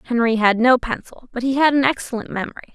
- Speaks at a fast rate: Yes, fast, 220 wpm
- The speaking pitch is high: Yes, high, 245 Hz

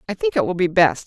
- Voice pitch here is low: No, high, 190 Hz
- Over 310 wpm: Yes, fast, 340 wpm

